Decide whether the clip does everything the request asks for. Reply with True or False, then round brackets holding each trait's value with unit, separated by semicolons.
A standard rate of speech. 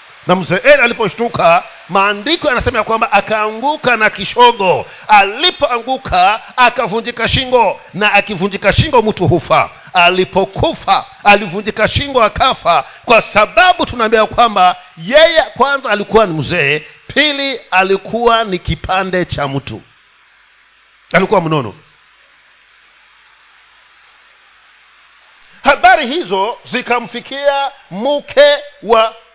False (90 wpm)